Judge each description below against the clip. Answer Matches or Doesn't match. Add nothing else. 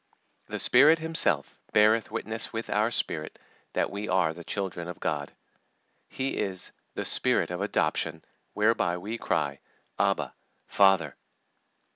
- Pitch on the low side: Matches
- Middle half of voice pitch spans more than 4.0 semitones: Matches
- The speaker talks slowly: Matches